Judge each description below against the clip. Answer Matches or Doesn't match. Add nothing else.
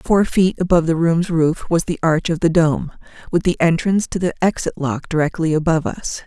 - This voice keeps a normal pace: Doesn't match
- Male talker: Doesn't match